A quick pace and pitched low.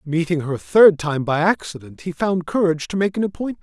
No: fast, 230 wpm; medium, 170 Hz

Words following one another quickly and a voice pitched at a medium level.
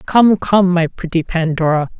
No: average, 150 wpm; medium, 175 Hz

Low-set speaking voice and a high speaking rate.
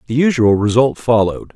No: low, 120 Hz; average, 155 wpm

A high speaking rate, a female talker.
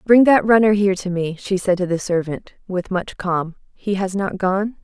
Yes: fast, 225 wpm; female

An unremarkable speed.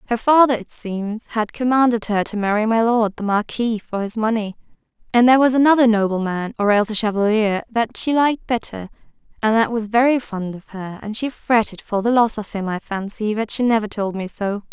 No: fast, 210 wpm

